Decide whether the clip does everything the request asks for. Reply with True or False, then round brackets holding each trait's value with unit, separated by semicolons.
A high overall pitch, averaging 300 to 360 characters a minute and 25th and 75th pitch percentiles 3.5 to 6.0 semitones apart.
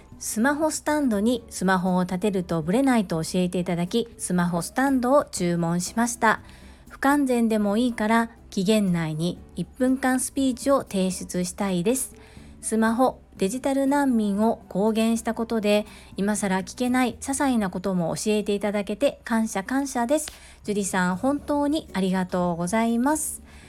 True (220 Hz; 325 characters per minute; 5.3 semitones)